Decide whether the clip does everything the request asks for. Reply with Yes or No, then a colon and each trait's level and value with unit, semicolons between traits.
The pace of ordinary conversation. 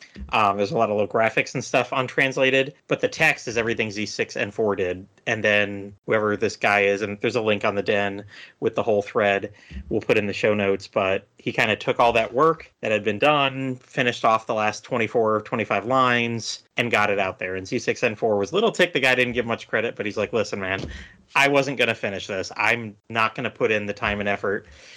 No: fast, 230 wpm